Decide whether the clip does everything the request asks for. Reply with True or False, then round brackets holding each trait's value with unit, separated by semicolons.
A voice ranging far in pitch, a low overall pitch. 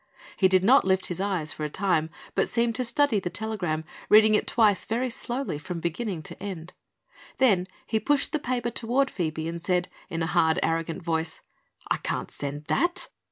False (6.1 semitones; 190 Hz)